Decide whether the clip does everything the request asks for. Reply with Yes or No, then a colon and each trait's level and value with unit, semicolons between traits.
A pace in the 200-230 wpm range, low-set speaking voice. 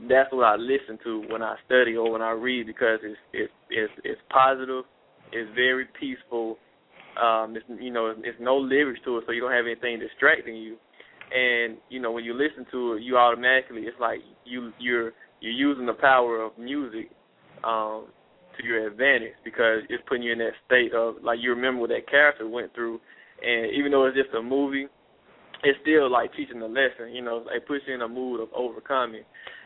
Yes: fast, 205 wpm; low, 120 Hz